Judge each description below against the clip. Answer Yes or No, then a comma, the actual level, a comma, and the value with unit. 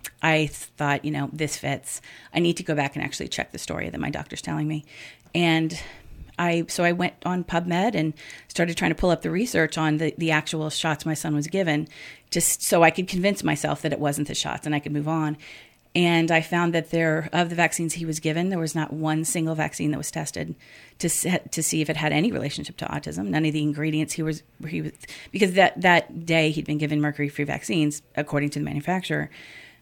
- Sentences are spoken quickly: Yes, fast, 225 wpm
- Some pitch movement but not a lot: No, narrow, 2.1 semitones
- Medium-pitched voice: Yes, medium, 160 Hz